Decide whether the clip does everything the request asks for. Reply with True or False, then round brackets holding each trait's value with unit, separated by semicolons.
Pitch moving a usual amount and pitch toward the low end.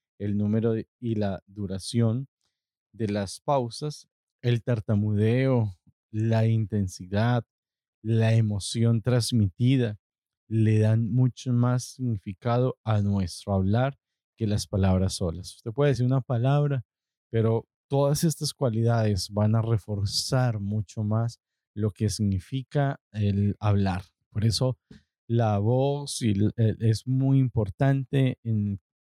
True (3.3 semitones; 110 Hz)